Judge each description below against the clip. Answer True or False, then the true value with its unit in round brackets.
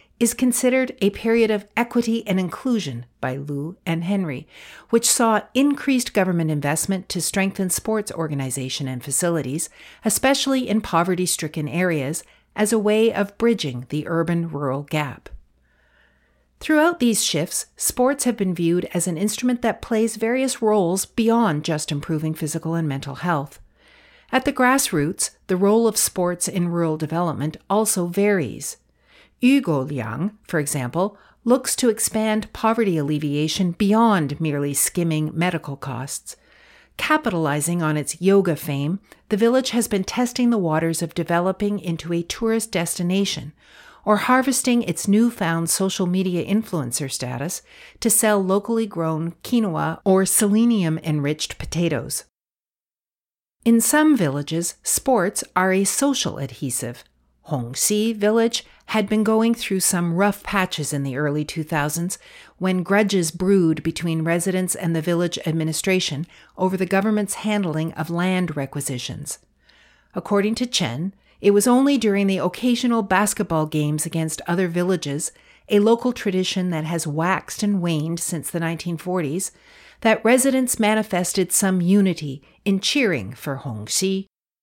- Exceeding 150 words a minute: False (135 wpm)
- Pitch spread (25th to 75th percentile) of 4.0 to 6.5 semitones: True (5.6 semitones)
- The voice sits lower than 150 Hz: False (185 Hz)